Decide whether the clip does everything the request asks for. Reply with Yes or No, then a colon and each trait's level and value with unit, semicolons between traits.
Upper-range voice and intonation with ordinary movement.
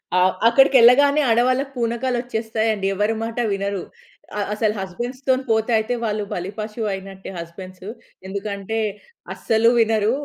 Yes: high, 220 Hz; average, 3.2 semitones